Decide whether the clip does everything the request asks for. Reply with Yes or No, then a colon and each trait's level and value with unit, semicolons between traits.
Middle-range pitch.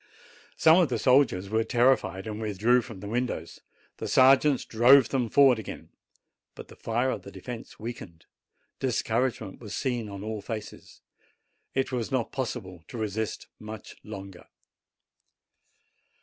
No: low, 115 Hz